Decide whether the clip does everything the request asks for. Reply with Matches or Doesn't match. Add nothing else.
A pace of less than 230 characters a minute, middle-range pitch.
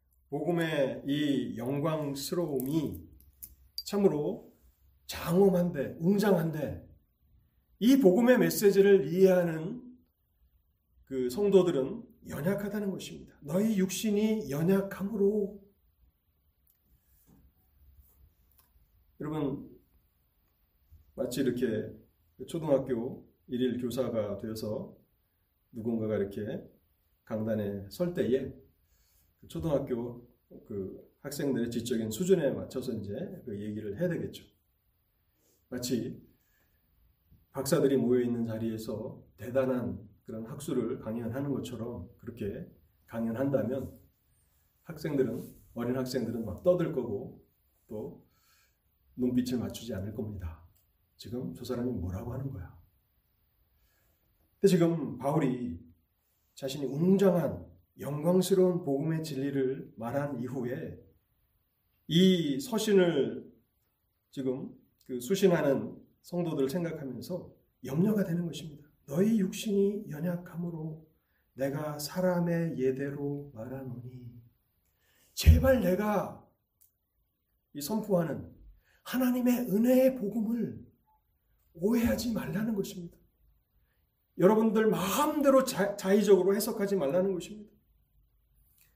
Doesn't match